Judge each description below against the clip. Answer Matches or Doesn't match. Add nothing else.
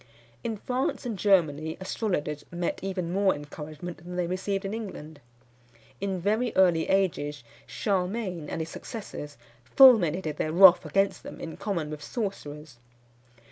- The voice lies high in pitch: Doesn't match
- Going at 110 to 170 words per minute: Matches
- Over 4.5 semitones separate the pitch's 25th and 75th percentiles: Doesn't match